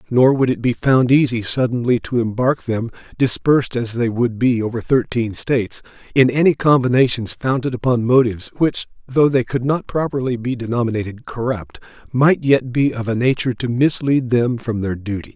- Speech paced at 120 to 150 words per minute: No, average, 175 wpm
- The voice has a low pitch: Yes, low, 125 Hz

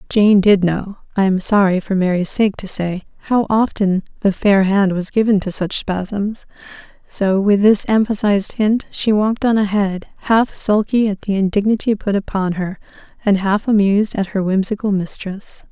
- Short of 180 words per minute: Yes, average, 170 wpm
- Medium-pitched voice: No, high, 200 Hz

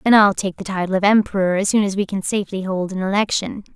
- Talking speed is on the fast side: Yes, fast, 255 wpm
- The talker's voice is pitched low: No, high, 195 Hz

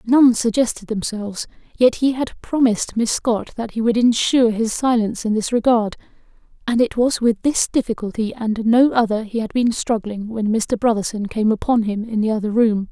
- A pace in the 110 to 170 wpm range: No, average, 190 wpm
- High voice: Yes, high, 225 Hz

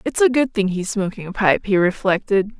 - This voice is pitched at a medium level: No, high, 200 Hz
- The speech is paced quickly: Yes, fast, 230 wpm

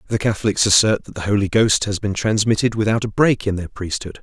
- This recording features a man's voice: Yes, male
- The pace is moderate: No, fast, 225 wpm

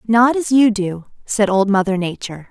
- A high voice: Yes, high, 210 Hz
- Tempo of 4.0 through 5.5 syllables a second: Yes, 5.1 syllables/s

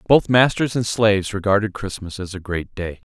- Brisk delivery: No, average, 195 wpm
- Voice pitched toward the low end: Yes, low, 100 Hz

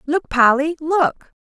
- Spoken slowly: Yes, slow, 125 wpm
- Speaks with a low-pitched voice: No, very high, 305 Hz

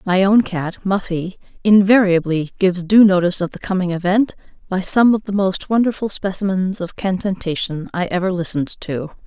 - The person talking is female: Yes, female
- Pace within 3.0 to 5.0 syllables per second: No, 5.3 syllables/s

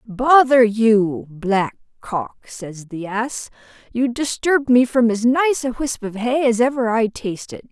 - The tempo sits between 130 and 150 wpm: No, average, 165 wpm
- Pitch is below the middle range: No, high, 235 Hz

